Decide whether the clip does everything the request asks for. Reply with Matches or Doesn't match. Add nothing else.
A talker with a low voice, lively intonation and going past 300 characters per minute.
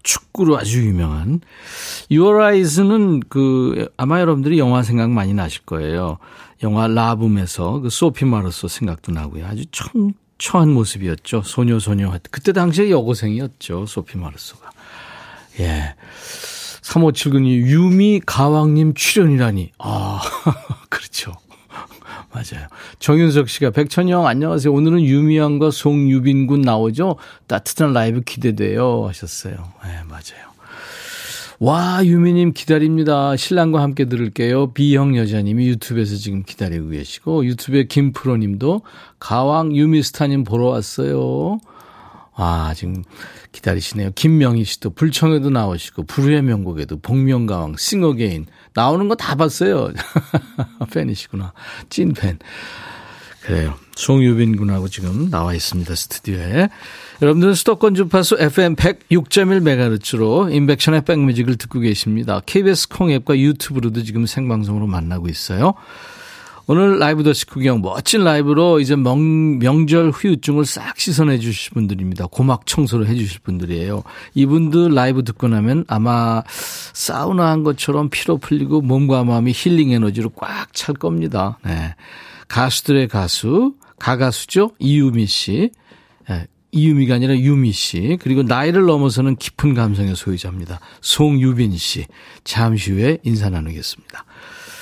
Matches